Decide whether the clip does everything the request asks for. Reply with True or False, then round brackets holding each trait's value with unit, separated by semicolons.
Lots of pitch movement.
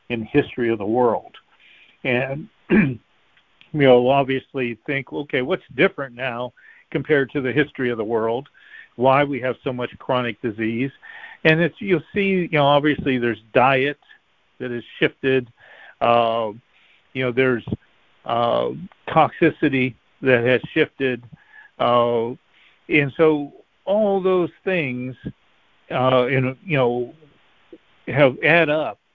False (3.8 semitones)